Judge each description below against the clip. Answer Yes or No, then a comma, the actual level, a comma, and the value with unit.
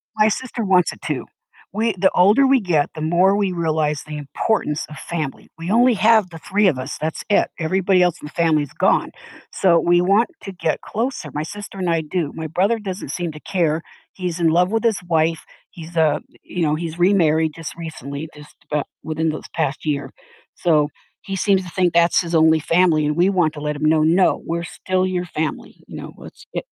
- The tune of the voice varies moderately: Yes, average, 3.3 semitones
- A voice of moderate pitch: Yes, medium, 170 Hz